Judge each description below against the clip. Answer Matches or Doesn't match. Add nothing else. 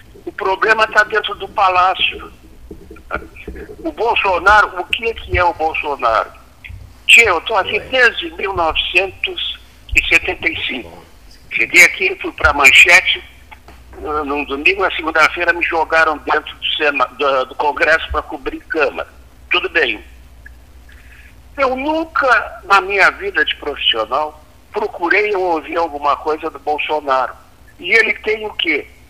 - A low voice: Doesn't match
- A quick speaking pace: Doesn't match